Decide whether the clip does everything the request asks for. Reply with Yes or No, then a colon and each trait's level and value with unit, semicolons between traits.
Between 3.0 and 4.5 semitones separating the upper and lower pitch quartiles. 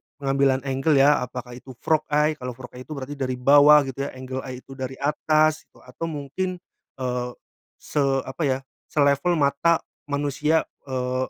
No: narrow, 2.5 semitones